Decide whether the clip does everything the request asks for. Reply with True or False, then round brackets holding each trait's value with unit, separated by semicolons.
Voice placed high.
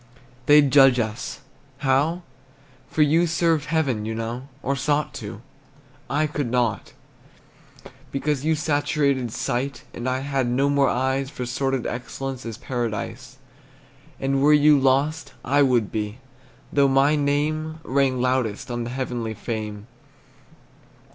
False (135 Hz)